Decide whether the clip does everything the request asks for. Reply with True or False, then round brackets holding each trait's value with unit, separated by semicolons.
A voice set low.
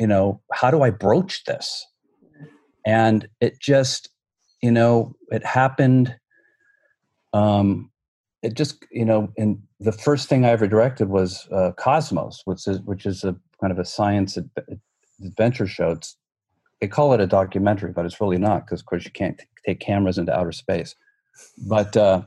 True (110 Hz)